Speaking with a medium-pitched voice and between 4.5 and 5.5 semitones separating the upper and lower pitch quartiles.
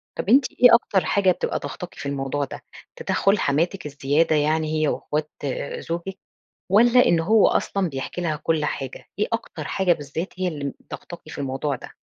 Yes: medium, 160 Hz; average, 4.8 semitones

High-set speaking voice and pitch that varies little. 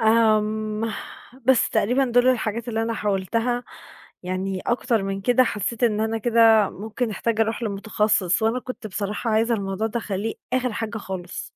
Yes: high, 220 Hz; narrow, 2.1 semitones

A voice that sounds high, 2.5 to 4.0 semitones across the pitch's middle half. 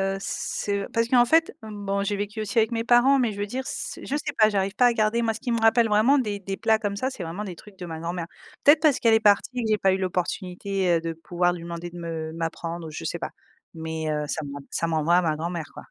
No: high, 200 Hz; average, 4.8 semitones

